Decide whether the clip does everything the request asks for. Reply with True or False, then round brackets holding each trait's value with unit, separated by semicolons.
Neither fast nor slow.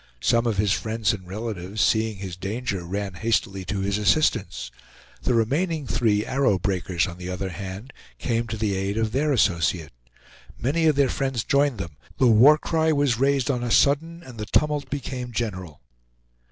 True (180 wpm)